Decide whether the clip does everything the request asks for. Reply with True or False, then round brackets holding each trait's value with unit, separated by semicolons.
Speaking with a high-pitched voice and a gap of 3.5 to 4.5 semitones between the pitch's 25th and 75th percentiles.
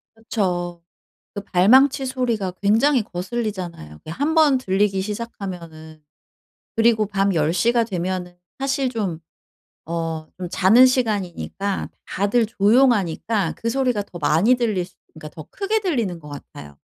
False (200 Hz; 5.2 semitones)